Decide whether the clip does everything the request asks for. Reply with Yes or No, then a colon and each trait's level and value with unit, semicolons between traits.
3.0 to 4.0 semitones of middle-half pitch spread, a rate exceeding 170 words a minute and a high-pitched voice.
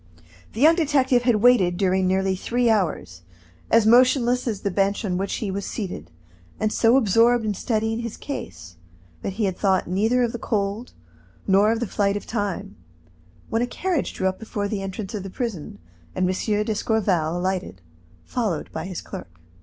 Yes: average, 3.7 semitones; average, 180 wpm; high, 205 Hz